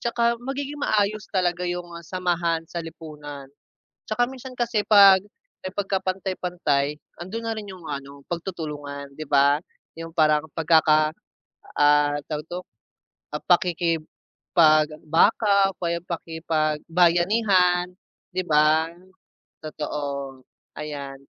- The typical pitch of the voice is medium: Yes, medium, 170 Hz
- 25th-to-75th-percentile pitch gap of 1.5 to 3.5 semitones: No, average, 3.9 semitones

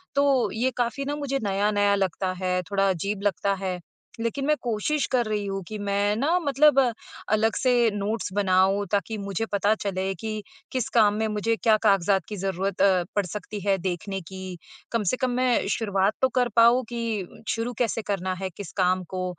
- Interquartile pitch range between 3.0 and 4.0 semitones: Yes, average, 3.3 semitones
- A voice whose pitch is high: Yes, high, 205 Hz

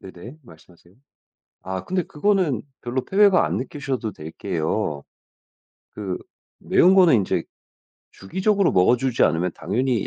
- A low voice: Yes, low, 120 Hz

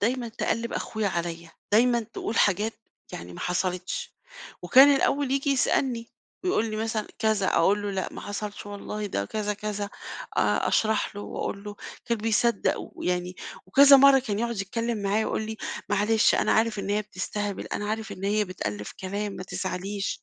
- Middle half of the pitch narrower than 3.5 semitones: Yes, narrow, 2.6 semitones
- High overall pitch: Yes, high, 210 Hz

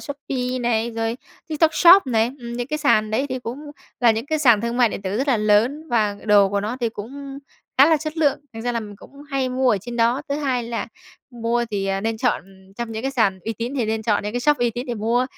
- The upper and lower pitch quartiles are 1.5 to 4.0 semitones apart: Yes, average, 3.5 semitones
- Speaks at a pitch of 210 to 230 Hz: No, high, 240 Hz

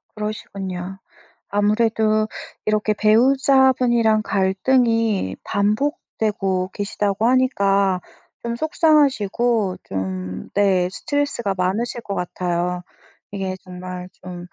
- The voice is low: No, high, 205 Hz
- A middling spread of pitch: Yes, average, 4.0 semitones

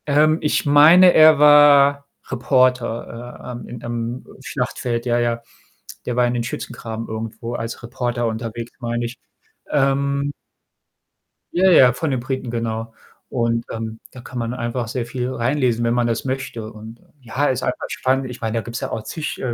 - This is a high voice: No, low, 120 Hz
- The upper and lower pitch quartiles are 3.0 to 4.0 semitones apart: No, narrow, 2.6 semitones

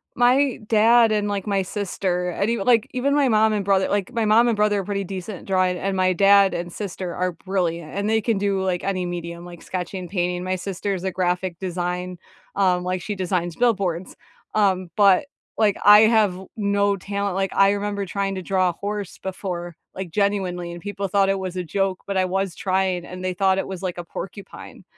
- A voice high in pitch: Yes, high, 195 Hz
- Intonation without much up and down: Yes, narrow, 2.0 semitones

